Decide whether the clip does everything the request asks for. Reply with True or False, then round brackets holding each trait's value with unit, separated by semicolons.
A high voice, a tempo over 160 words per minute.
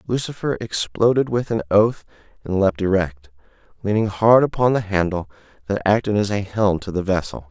False (100 Hz; 170 wpm)